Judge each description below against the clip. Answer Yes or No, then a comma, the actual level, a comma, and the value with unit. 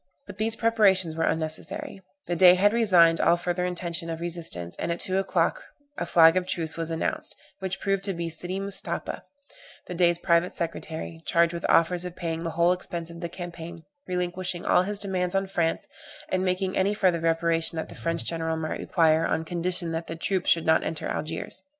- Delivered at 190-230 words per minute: Yes, average, 195 wpm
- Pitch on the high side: No, medium, 175 Hz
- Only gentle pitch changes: Yes, narrow, 2.1 semitones